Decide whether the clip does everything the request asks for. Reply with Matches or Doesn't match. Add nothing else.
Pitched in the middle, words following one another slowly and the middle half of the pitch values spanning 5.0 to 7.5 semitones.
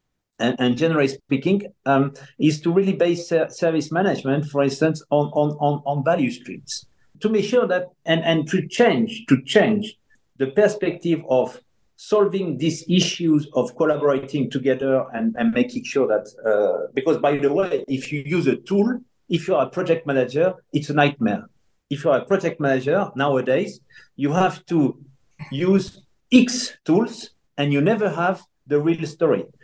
Doesn't match